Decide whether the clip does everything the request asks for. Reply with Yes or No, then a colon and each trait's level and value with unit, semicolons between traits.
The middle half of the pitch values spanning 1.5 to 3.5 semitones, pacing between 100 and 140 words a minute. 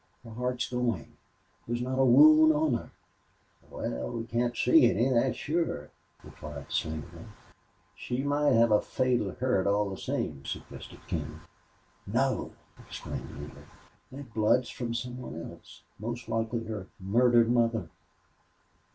Yes: average, 3.0 semitones; slow, 135 wpm